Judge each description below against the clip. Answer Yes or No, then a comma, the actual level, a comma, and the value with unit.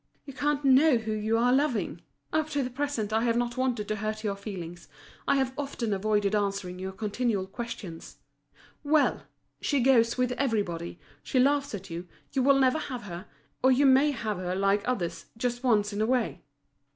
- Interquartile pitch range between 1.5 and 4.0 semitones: No, average, 4.5 semitones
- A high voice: Yes, high, 230 Hz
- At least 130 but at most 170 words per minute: No, average, 190 wpm